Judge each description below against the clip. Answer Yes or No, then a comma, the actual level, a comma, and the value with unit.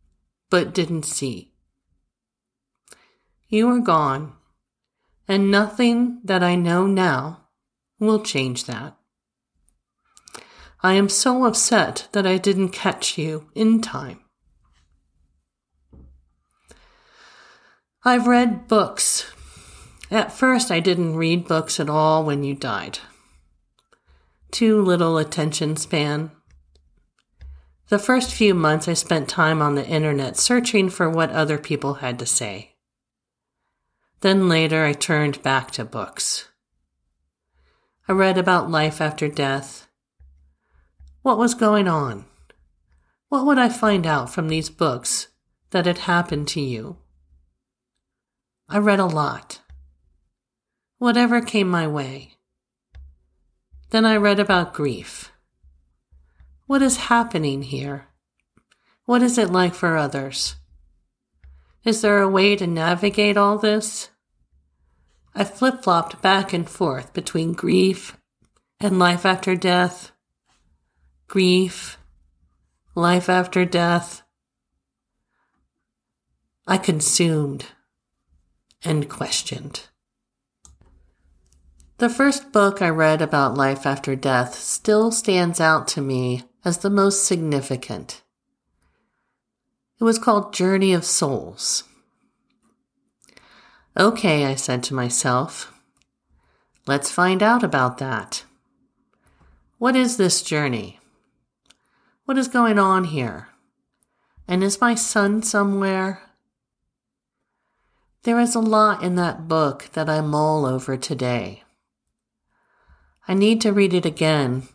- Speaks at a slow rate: Yes, slow, 110 wpm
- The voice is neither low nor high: Yes, medium, 160 Hz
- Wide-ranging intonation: Yes, wide, 8.7 semitones